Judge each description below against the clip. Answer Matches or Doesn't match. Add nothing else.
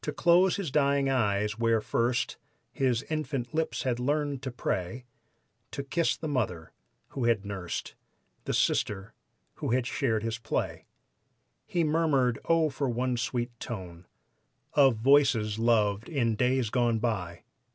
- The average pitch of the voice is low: Matches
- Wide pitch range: Doesn't match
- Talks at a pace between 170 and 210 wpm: Doesn't match